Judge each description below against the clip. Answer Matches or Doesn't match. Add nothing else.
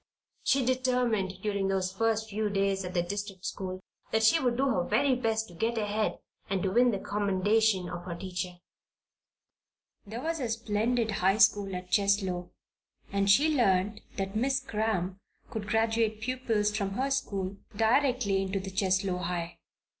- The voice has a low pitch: Doesn't match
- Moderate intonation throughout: Matches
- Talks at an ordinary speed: Matches